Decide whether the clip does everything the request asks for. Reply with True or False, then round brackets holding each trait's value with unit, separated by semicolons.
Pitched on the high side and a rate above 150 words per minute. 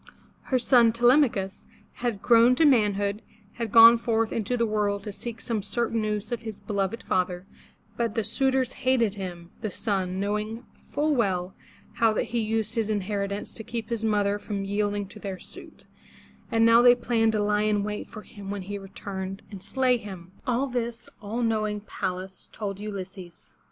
True (215 Hz; 185 wpm)